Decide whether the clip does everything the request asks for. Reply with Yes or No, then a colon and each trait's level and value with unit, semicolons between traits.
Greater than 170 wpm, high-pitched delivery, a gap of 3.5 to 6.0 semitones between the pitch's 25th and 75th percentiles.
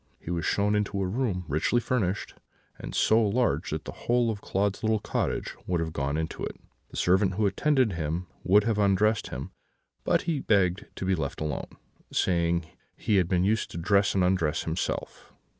No: average, 190 wpm; very low, 95 Hz; average, 3.9 semitones